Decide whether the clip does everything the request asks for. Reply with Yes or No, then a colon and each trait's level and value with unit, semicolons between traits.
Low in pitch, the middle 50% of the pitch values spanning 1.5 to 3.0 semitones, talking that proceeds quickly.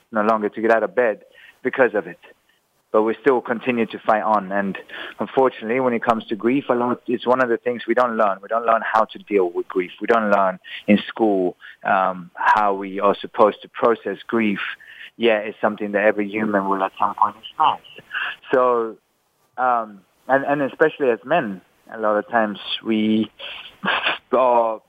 No: low, 110 Hz; narrow, 2.6 semitones; average, 195 wpm